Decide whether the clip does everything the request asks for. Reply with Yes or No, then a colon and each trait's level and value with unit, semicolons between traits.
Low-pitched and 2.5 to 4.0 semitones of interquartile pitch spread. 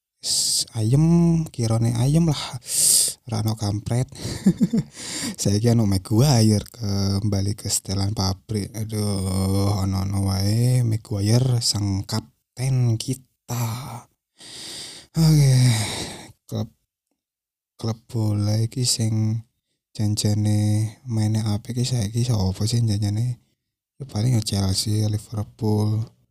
Yes: low, 110 Hz; average, 2.8 semitones